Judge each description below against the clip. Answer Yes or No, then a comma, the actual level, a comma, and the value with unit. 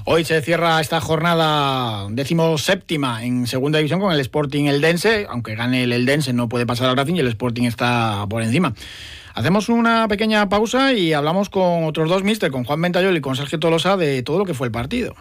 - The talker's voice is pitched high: No, medium, 150 Hz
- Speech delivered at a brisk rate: Yes, fast, 215 wpm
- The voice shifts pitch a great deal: Yes, wide, 5.9 semitones